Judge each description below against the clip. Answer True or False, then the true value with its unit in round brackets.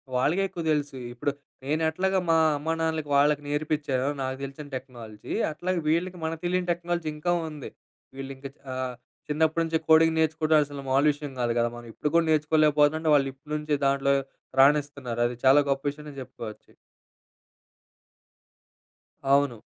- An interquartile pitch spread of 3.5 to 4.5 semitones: False (2.8 semitones)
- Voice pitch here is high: False (150 Hz)